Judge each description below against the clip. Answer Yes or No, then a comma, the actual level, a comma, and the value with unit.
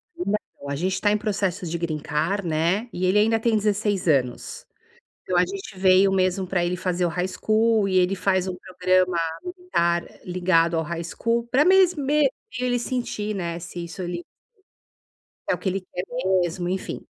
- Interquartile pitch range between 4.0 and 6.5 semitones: No, average, 3.3 semitones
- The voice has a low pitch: No, medium, 185 Hz